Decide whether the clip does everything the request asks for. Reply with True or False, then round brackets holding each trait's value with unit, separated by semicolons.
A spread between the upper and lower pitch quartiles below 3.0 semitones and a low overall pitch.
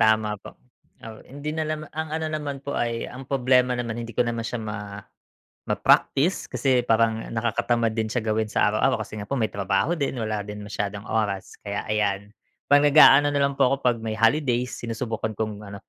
False (4.0 semitones; 115 Hz)